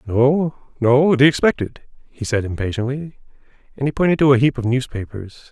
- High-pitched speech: No, low, 130 Hz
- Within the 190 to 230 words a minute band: No, average, 165 wpm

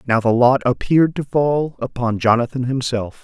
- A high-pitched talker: No, low, 125 Hz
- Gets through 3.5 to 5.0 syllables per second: Yes, 4.9 syllables/s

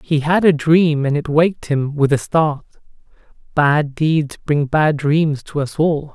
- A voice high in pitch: No, medium, 150 Hz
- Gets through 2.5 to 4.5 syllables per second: Yes, 3.9 syllables/s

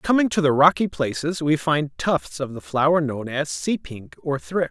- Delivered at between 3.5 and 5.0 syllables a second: Yes, 4.6 syllables/s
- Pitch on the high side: No, medium, 150 Hz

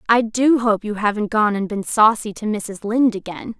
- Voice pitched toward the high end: Yes, high, 215 Hz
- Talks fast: Yes, fast, 215 wpm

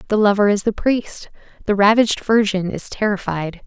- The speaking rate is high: No, average, 165 wpm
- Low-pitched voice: No, high, 205 Hz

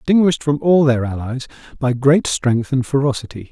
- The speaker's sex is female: No, male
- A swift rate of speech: No, average, 170 wpm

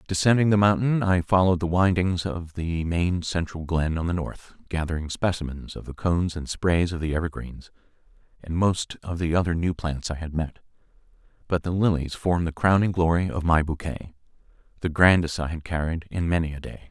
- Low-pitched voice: Yes, very low, 85 Hz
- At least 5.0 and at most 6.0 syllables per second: Yes, 5.4 syllables/s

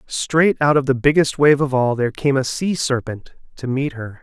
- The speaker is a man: Yes, male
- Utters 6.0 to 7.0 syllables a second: No, 4.9 syllables/s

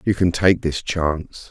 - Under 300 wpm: Yes, average, 200 wpm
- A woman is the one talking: No, male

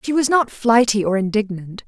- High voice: Yes, high, 220 Hz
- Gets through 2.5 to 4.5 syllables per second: No, 5.2 syllables/s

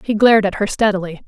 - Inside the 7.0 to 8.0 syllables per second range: Yes, 7.1 syllables/s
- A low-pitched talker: No, high, 205 Hz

